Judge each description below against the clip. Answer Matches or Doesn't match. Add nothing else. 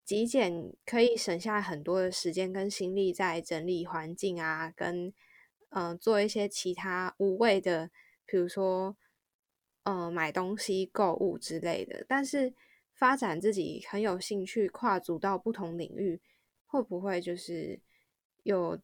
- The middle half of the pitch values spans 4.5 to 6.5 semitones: Doesn't match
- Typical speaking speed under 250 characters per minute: Matches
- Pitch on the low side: Doesn't match